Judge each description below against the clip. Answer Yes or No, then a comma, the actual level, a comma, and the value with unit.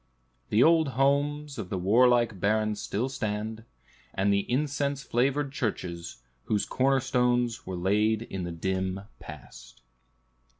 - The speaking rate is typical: No, slow, 130 wpm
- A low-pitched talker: Yes, low, 110 Hz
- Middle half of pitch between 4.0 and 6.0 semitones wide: Yes, wide, 5.6 semitones